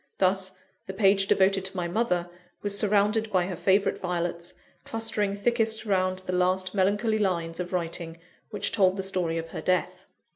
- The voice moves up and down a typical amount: No, narrow, 2.1 semitones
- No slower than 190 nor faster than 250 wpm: No, average, 170 wpm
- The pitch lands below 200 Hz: Yes, high, 190 Hz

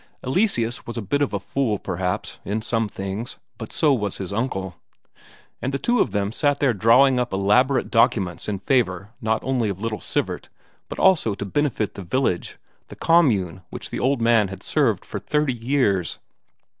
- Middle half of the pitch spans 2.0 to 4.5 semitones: No, average, 5.1 semitones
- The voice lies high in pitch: No, low, 115 Hz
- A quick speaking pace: No, average, 180 wpm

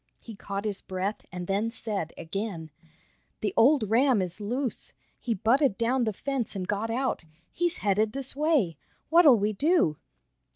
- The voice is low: No, high, 220 Hz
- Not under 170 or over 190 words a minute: No, average, 160 wpm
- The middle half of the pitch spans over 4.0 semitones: Yes, average, 5.1 semitones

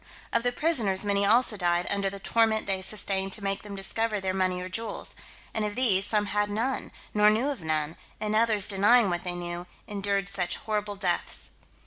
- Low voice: No, high, 200 Hz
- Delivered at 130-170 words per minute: No, average, 195 wpm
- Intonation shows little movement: Yes, narrow, 2.3 semitones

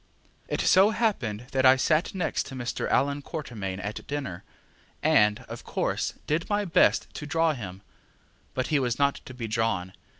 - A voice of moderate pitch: No, low, 130 Hz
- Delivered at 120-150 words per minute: No, average, 170 wpm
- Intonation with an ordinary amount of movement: No, wide, 5.9 semitones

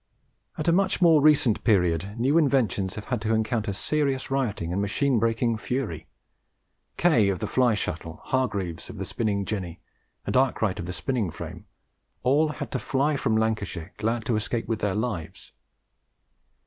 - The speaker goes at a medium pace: Yes, average, 165 wpm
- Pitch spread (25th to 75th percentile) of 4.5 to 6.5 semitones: Yes, average, 5.0 semitones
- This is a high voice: No, low, 110 Hz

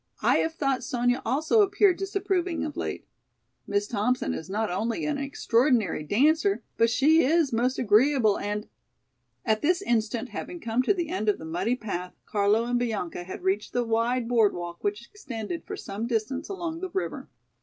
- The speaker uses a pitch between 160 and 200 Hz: No, high, 240 Hz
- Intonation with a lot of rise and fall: Yes, wide, 6.8 semitones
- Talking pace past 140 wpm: Yes, average, 175 wpm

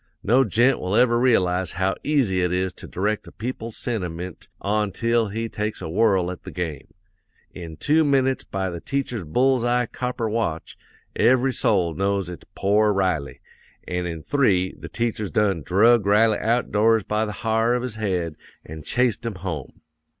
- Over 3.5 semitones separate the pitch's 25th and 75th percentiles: Yes, average, 4.4 semitones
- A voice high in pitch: No, low, 105 Hz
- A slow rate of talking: No, average, 170 wpm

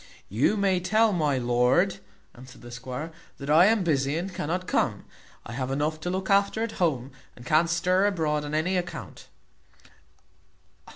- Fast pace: No, average, 165 wpm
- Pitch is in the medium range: Yes, medium, 160 Hz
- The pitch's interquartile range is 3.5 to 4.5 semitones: No, wide, 5.4 semitones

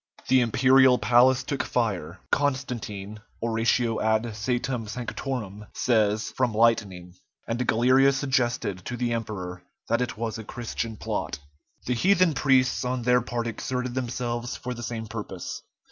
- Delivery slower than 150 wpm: Yes, average, 140 wpm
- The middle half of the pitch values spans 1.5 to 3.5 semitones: Yes, narrow, 2.4 semitones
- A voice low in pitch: Yes, low, 120 Hz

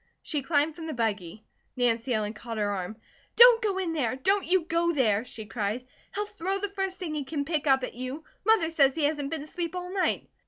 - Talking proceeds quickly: Yes, fast, 225 wpm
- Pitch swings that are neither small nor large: No, wide, 6.9 semitones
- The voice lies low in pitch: No, very high, 300 Hz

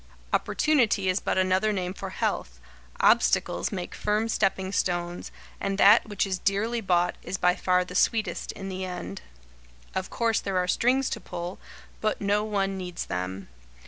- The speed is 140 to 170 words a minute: Yes, average, 165 wpm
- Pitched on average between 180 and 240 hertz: Yes, high, 190 Hz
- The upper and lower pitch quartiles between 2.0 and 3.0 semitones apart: Yes, narrow, 2.6 semitones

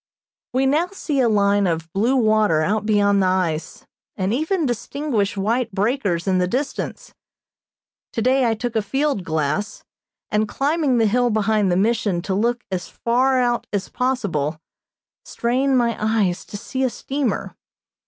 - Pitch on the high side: Yes, high, 220 Hz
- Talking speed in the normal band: Yes, average, 155 wpm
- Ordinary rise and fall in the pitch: Yes, average, 4.5 semitones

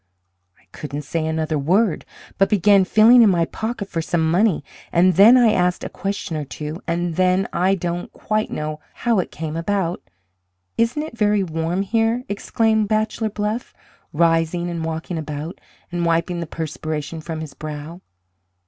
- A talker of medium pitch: Yes, medium, 175 Hz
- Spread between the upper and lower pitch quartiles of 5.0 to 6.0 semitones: No, average, 4.4 semitones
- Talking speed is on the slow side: No, average, 165 wpm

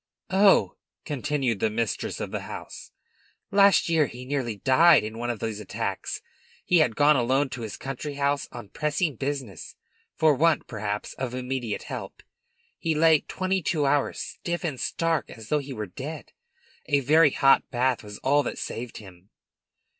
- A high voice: No, low, 135 Hz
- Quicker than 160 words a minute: Yes, average, 170 wpm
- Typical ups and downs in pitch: Yes, average, 4.5 semitones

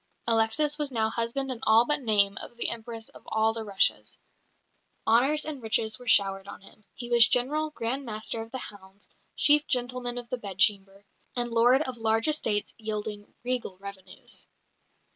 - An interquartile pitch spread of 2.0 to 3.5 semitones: Yes, average, 3.1 semitones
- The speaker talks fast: No, average, 165 wpm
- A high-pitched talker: Yes, high, 230 Hz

